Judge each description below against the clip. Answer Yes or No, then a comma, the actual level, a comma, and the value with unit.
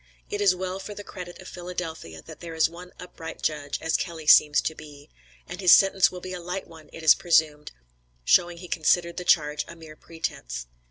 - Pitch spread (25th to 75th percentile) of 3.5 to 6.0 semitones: No, average, 2.8 semitones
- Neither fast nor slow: No, fast, 210 wpm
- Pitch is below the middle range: No, medium, 170 Hz